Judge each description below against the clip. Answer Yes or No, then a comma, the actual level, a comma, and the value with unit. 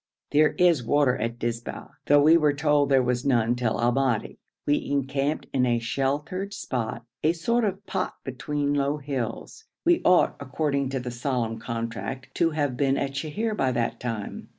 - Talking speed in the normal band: Yes, average, 175 wpm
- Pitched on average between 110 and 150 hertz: Yes, low, 135 Hz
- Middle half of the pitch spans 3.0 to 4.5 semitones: Yes, average, 3.4 semitones